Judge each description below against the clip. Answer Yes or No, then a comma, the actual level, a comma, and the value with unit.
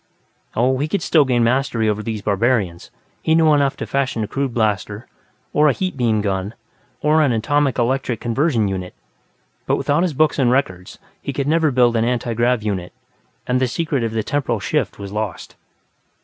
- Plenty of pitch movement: No, average, 4.5 semitones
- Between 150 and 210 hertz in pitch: No, low, 120 Hz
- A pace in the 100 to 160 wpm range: No, average, 185 wpm